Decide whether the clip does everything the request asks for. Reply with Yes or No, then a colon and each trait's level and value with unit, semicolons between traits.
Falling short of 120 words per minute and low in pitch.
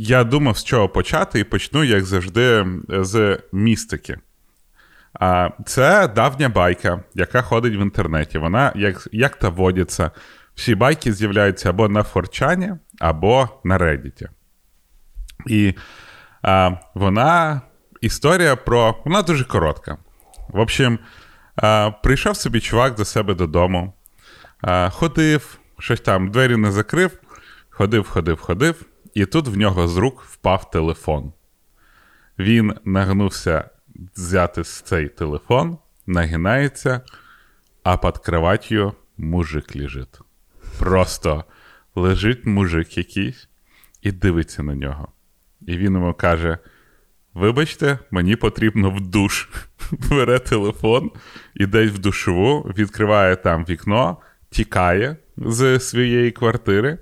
Yes: average, 110 wpm; low, 100 Hz